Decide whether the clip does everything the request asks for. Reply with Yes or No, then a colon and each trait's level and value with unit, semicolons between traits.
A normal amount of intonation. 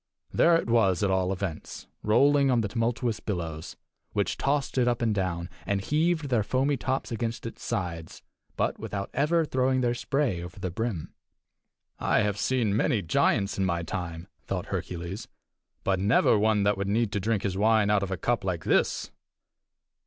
Yes: average, 4.3 semitones